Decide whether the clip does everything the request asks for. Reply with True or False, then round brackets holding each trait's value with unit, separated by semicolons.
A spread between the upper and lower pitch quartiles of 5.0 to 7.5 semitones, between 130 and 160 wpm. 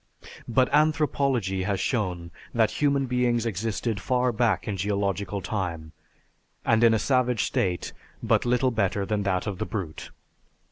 False (4.3 semitones; 145 wpm)